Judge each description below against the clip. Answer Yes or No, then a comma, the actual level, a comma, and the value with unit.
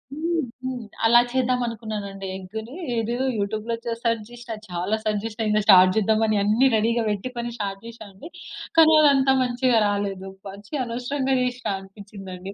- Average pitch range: Yes, average, 3.4 semitones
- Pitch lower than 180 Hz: No, high, 220 Hz